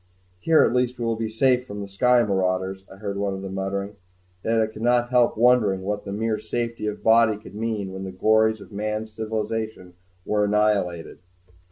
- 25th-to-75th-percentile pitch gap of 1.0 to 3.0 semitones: Yes, narrow, 2.5 semitones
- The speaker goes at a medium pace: No, fast, 210 wpm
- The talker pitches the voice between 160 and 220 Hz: No, low, 105 Hz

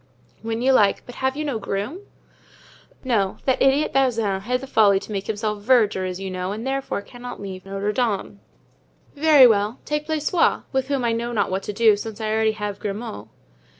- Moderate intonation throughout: Yes, average, 4.5 semitones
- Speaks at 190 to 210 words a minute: Yes, average, 195 wpm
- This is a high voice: Yes, high, 225 Hz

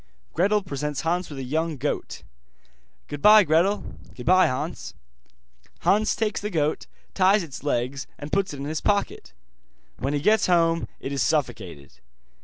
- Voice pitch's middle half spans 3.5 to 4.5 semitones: No, wide, 5.5 semitones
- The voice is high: No, medium, 160 Hz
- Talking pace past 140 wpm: Yes, average, 150 wpm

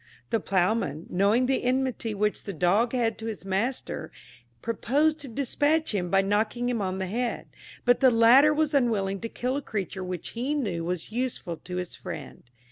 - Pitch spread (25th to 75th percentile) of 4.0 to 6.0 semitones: Yes, average, 4.8 semitones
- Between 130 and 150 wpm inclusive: No, average, 185 wpm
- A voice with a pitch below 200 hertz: No, high, 225 Hz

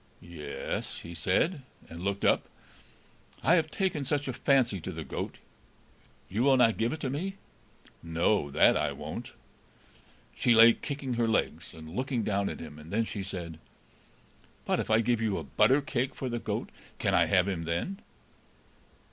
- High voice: No, low, 110 Hz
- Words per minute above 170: Yes, average, 180 wpm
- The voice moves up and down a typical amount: No, wide, 7.4 semitones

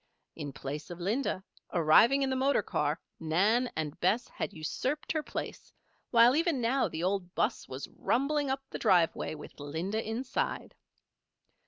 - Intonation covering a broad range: Yes, wide, 8.5 semitones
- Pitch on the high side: Yes, high, 210 Hz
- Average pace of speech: Yes, average, 155 wpm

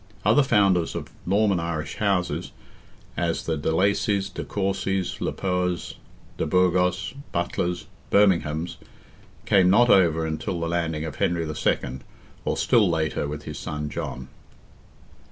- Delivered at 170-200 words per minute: No, slow, 135 wpm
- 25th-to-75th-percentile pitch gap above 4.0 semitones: No, average, 3.3 semitones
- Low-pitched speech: Yes, very low, 85 Hz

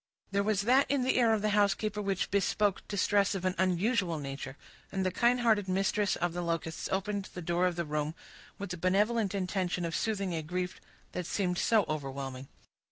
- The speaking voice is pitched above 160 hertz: Yes, high, 190 Hz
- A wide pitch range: No, average, 3.1 semitones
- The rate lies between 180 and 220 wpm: Yes, average, 195 wpm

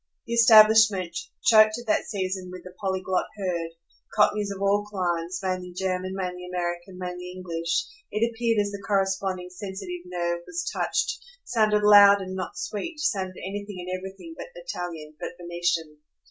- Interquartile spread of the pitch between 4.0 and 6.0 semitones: No, narrow, 2.6 semitones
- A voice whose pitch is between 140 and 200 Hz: Yes, high, 190 Hz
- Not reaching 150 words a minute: No, average, 155 wpm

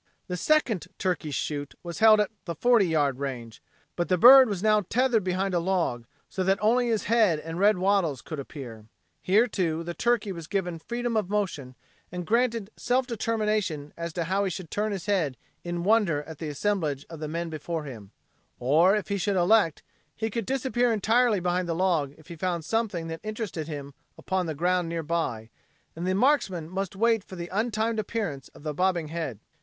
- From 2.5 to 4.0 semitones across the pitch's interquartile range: No, average, 4.9 semitones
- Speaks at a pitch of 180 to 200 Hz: Yes, medium, 185 Hz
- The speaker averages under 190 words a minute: No, average, 195 wpm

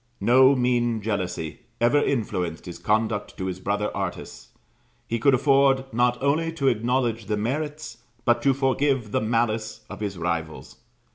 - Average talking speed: Yes, average, 150 wpm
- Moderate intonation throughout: Yes, average, 4.3 semitones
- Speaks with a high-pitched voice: No, low, 120 Hz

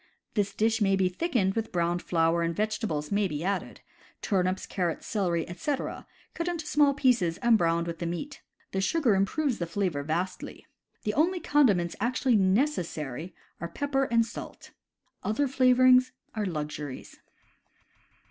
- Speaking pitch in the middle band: No, high, 200 Hz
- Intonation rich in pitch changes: Yes, wide, 6.9 semitones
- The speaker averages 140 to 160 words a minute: Yes, average, 150 wpm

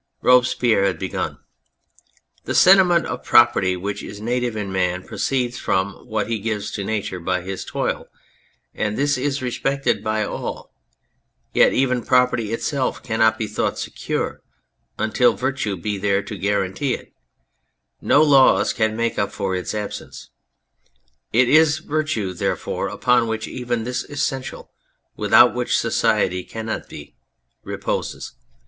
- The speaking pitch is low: Yes, low, 110 Hz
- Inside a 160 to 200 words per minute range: No, average, 140 wpm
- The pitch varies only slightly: No, average, 4.1 semitones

